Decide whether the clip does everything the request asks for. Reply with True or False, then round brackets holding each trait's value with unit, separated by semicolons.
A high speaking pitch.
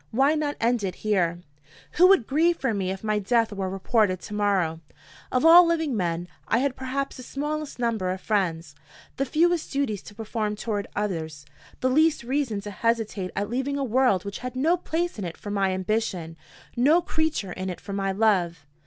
True (220 Hz)